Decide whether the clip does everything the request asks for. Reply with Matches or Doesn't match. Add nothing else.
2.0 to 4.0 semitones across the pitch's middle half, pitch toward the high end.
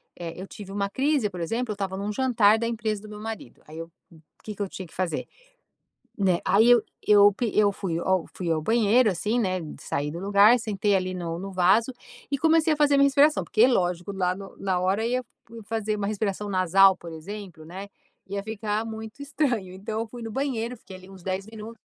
Matches